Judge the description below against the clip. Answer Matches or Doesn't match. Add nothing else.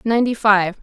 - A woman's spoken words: Matches